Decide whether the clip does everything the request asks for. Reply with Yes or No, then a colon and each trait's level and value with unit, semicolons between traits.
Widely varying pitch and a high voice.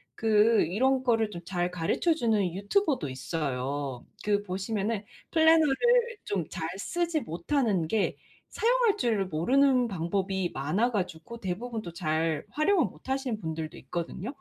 Yes: wide, 7.0 semitones; high, 205 Hz